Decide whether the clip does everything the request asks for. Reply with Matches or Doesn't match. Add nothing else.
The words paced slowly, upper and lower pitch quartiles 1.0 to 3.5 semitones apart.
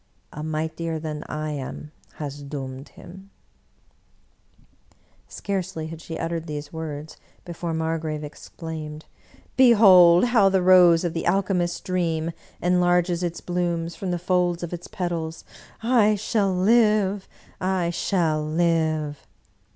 Matches